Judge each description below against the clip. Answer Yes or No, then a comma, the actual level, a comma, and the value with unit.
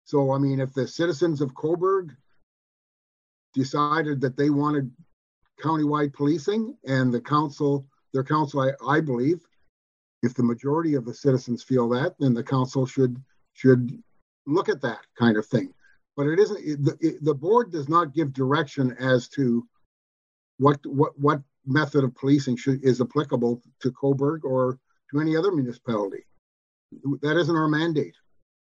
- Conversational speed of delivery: Yes, average, 155 wpm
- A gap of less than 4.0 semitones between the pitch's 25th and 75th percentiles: Yes, average, 3.2 semitones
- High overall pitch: No, medium, 140 Hz